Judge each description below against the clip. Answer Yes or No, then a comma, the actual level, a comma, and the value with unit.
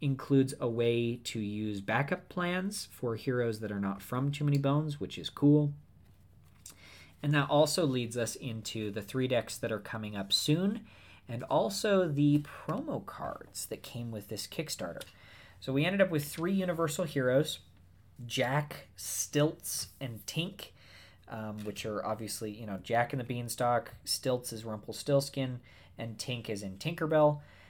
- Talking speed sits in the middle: Yes, average, 160 wpm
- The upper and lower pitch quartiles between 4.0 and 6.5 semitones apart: Yes, wide, 5.6 semitones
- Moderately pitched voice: No, low, 120 Hz